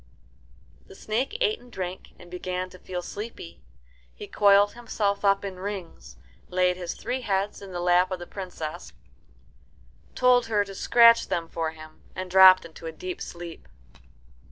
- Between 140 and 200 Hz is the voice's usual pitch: Yes, medium, 185 Hz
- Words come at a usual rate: Yes, average, 160 wpm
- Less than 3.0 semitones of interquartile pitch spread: Yes, narrow, 2.6 semitones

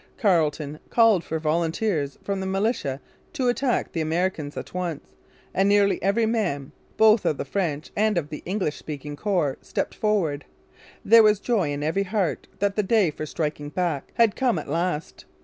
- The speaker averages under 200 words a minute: Yes, average, 175 wpm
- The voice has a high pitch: No, medium, 180 Hz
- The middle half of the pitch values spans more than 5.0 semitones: Yes, wide, 5.6 semitones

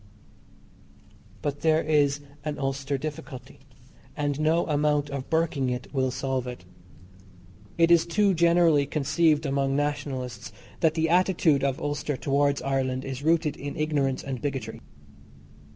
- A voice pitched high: No, medium, 145 Hz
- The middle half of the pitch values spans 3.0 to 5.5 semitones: No, narrow, 2.6 semitones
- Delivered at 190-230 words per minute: No, slow, 135 wpm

